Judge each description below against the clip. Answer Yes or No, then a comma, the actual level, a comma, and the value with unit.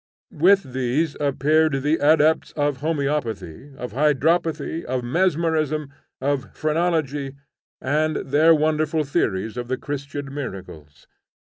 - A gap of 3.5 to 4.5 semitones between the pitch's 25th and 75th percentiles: No, average, 2.9 semitones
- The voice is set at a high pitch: No, medium, 145 Hz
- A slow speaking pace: Yes, slow, 110 wpm